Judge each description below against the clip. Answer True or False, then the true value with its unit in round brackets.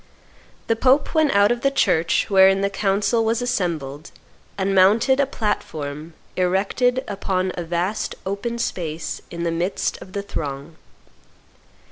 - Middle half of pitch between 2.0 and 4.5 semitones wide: False (5.1 semitones)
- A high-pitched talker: True (195 Hz)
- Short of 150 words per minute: True (140 wpm)